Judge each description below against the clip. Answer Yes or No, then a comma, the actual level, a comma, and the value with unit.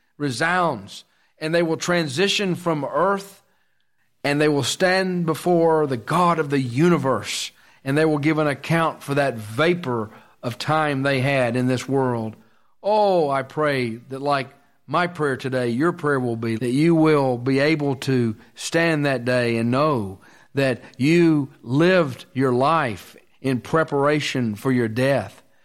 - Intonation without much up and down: No, average, 4.0 semitones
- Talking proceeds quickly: No, average, 155 wpm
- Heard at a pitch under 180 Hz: Yes, medium, 140 Hz